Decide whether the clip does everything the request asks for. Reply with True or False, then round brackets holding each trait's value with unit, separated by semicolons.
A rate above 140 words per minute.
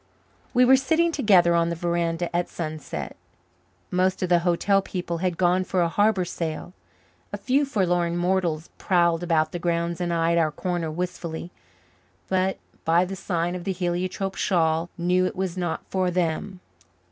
True (165 wpm)